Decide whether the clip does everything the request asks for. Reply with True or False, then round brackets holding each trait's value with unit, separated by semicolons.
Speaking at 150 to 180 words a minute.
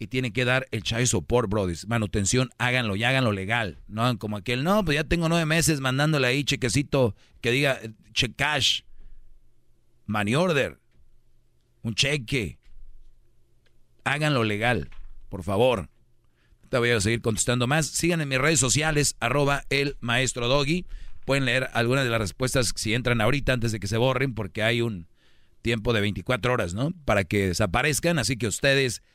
True (165 wpm)